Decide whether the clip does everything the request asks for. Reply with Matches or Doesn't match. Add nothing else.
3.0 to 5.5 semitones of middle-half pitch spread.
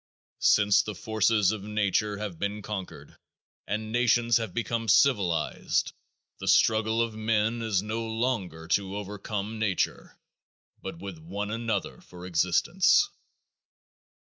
Doesn't match